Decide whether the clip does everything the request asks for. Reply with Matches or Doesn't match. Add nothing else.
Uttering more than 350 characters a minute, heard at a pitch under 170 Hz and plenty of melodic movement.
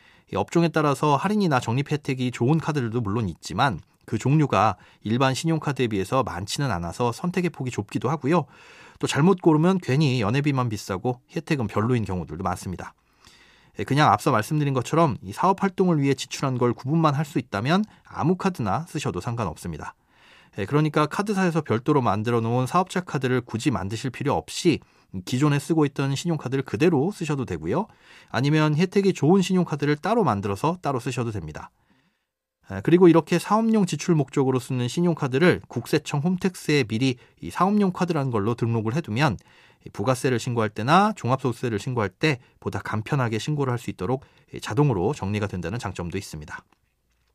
Matches